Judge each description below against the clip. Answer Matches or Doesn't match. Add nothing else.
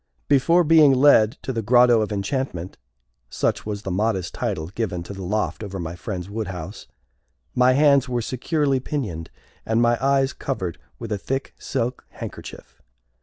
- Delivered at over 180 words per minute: Doesn't match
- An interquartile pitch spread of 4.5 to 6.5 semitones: Matches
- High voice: Doesn't match